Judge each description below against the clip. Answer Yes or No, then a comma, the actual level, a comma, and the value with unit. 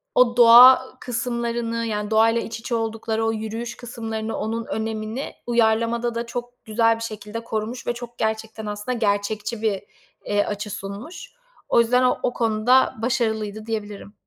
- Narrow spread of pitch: Yes, narrow, 1.5 semitones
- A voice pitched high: Yes, high, 225 Hz